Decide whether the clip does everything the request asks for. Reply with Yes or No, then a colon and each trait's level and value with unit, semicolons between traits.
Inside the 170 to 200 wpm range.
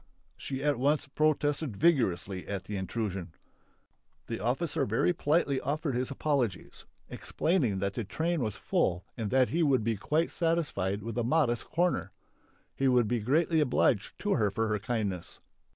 No: average, 160 wpm